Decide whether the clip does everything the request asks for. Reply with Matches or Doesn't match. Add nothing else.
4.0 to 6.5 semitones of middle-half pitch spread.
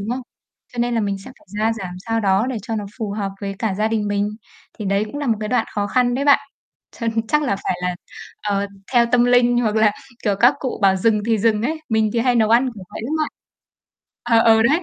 Doesn't match